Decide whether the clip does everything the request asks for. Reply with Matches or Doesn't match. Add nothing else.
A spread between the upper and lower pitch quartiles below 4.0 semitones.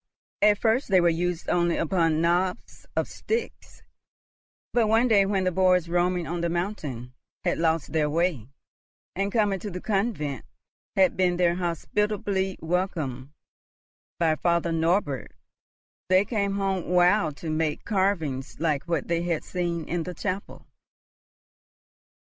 Matches